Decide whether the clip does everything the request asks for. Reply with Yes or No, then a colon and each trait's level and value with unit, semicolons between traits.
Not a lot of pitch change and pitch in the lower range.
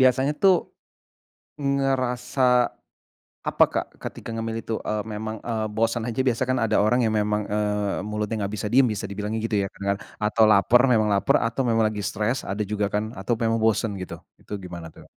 Yes: narrow, 2.1 semitones; low, 110 Hz